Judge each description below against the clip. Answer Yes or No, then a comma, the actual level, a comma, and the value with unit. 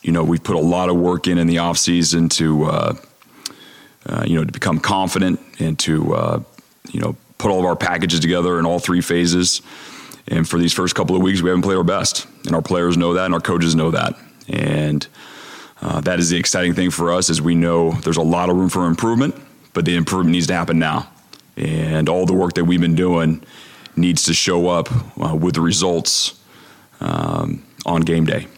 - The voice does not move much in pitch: Yes, narrow, 1.4 semitones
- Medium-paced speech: No, fast, 215 wpm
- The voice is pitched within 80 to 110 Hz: Yes, very low, 85 Hz